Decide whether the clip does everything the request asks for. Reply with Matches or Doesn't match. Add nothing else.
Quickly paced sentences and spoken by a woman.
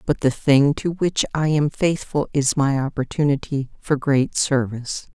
Doesn't match